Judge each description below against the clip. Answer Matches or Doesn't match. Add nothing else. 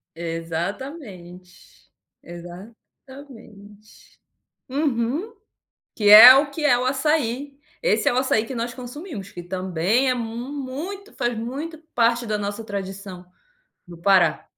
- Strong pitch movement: Matches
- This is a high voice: Matches